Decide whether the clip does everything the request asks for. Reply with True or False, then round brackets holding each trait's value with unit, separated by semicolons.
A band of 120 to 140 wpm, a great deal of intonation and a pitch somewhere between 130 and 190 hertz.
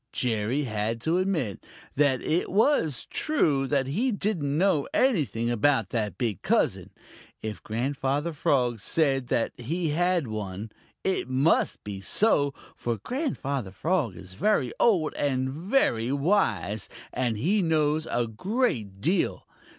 True (135 wpm; 7.0 semitones; 140 Hz)